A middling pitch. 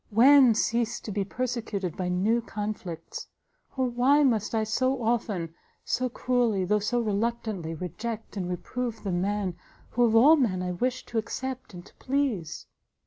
No: high, 220 Hz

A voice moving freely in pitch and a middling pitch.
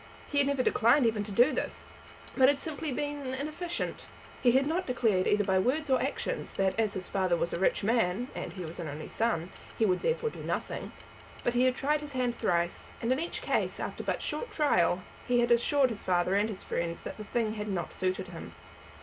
No: wide, 6.6 semitones; high, 235 Hz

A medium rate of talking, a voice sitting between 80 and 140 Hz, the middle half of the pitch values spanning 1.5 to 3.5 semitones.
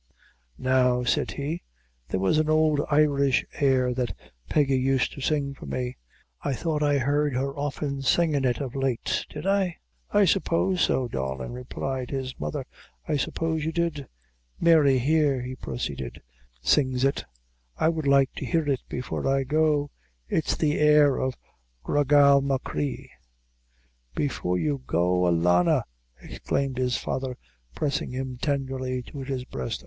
Yes: average, 150 wpm; low, 135 Hz; average, 2.7 semitones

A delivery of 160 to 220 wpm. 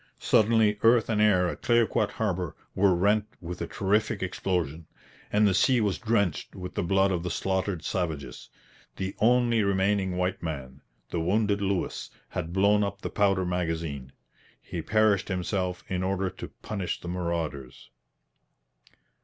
No: average, 150 wpm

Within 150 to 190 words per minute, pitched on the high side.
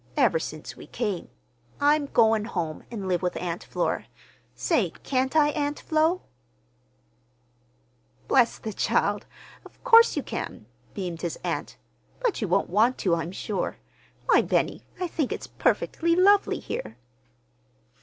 No: average, 140 wpm; high, 240 Hz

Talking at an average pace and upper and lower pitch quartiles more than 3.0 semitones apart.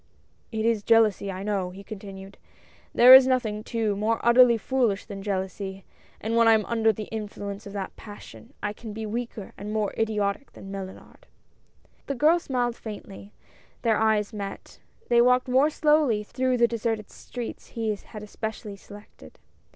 No: average, 165 wpm; average, 2.7 semitones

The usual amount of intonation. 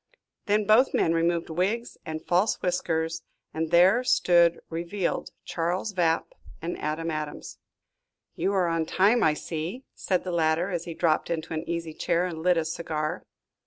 No: narrow, 2.1 semitones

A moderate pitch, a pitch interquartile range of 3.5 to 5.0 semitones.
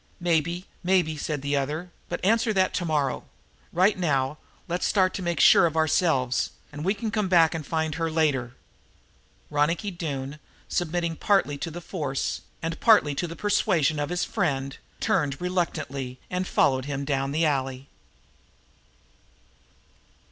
Yes: medium, 160 Hz; average, 3.9 semitones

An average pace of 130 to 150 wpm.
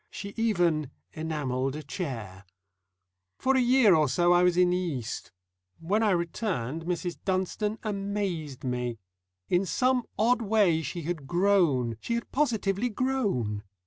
Yes: average, 145 wpm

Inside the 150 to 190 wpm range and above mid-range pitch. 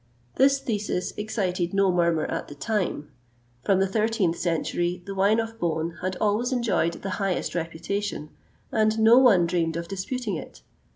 Yes: average, 160 wpm; high, 195 Hz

